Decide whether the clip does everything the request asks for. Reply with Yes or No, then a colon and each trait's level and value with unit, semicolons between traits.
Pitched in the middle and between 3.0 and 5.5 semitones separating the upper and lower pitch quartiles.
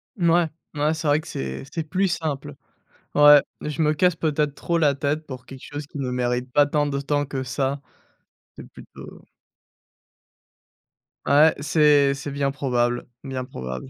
No: medium, 145 Hz; narrow, 2.4 semitones